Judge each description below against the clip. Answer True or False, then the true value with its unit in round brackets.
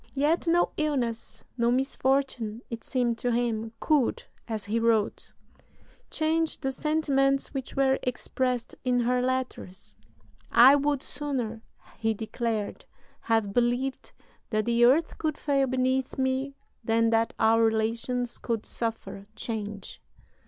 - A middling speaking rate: False (125 wpm)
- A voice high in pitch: True (245 Hz)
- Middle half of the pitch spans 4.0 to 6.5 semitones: False (3.0 semitones)